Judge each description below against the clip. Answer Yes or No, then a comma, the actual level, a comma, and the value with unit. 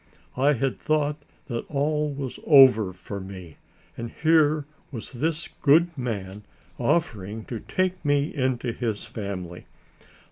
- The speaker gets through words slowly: Yes, slow, 130 wpm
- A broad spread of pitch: Yes, wide, 5.8 semitones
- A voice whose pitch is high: No, low, 130 Hz